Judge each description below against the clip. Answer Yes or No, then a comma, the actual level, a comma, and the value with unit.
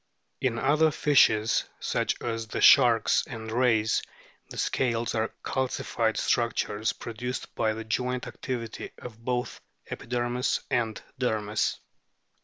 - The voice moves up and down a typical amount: No, narrow, 2.0 semitones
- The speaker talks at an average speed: No, slow, 115 wpm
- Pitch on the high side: No, low, 115 Hz